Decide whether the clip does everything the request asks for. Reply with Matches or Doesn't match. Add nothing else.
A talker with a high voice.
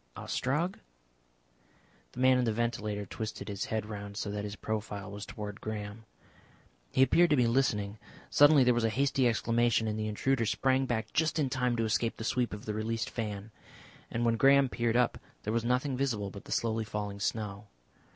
Doesn't match